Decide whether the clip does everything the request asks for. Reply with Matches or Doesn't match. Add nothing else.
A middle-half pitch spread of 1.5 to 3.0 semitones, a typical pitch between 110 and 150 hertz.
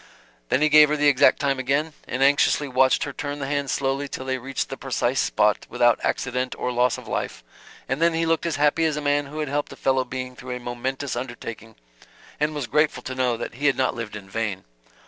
Matches